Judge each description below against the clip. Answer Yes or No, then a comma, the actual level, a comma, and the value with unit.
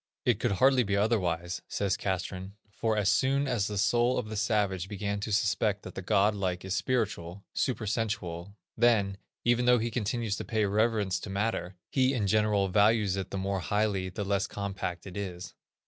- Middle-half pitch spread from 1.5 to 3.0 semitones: Yes, narrow, 2.5 semitones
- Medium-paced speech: Yes, average, 185 wpm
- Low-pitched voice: Yes, low, 100 Hz